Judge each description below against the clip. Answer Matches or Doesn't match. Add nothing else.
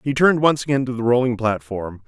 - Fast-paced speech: Matches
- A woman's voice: Doesn't match